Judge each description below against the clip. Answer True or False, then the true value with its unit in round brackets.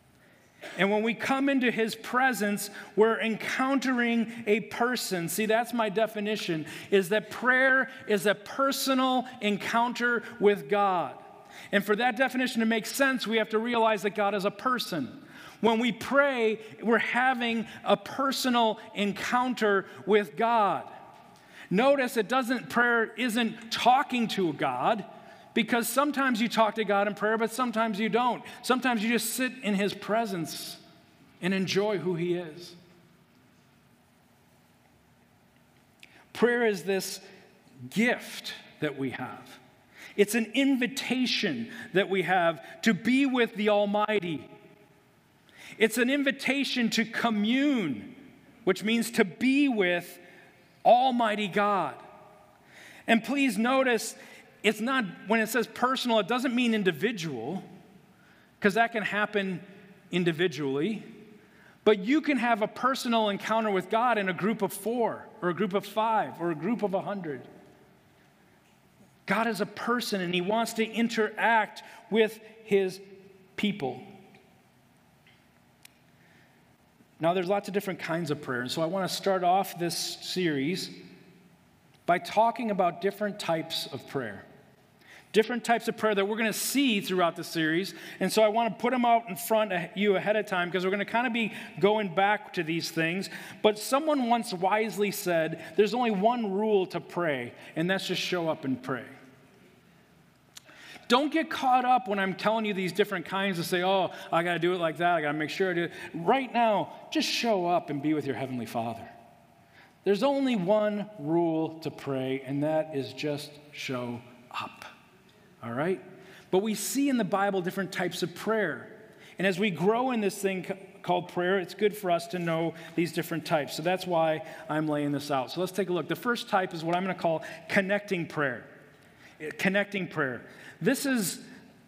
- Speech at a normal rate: True (165 wpm)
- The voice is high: True (205 Hz)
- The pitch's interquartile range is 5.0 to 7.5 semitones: False (4.5 semitones)